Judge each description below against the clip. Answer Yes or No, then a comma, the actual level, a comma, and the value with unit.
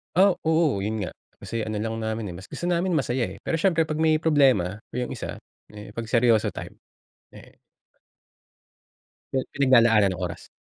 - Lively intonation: Yes, wide, 6.4 semitones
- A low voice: Yes, low, 120 Hz